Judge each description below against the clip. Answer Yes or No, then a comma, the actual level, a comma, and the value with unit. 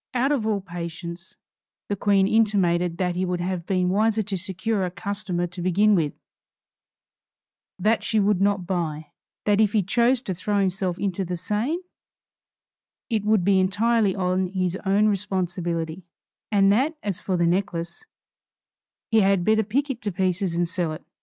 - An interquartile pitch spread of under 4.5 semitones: Yes, average, 2.9 semitones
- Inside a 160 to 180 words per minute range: Yes, average, 165 wpm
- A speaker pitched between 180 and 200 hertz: Yes, high, 190 Hz